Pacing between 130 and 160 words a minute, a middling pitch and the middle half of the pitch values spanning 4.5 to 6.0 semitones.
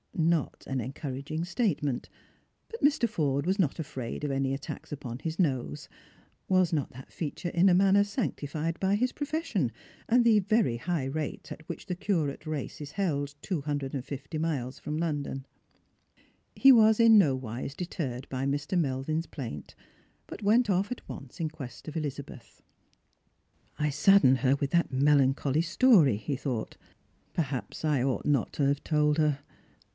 No: average, 170 wpm; medium, 150 Hz; average, 5.0 semitones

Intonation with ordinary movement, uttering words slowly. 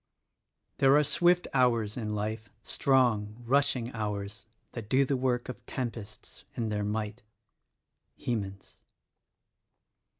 Yes: average, 3.5 semitones; slow, 120 wpm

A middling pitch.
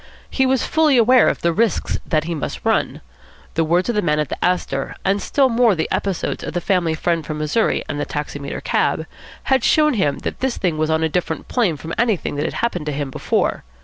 Yes: medium, 175 Hz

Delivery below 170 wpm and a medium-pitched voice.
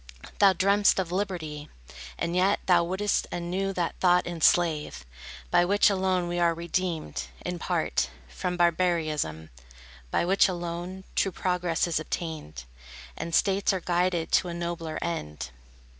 Yes: average, 140 wpm; medium, 175 Hz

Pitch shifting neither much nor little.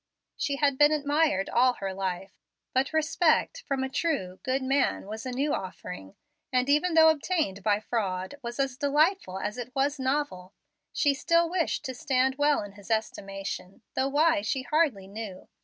No: wide, 6.5 semitones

